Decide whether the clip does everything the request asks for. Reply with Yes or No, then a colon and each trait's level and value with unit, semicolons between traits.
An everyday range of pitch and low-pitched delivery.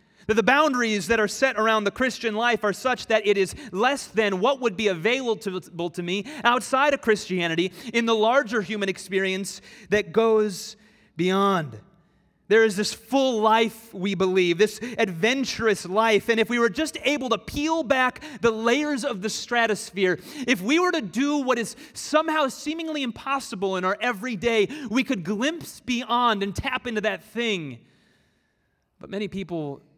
No: average, 4.3 semitones; high, 225 Hz